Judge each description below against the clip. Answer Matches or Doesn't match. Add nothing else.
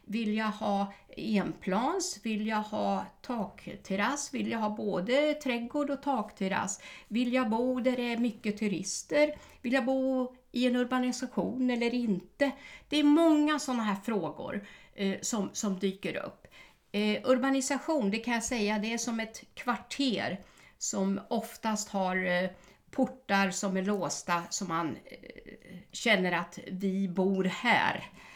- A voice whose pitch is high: Matches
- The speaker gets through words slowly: Doesn't match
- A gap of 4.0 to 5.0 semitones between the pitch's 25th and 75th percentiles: Matches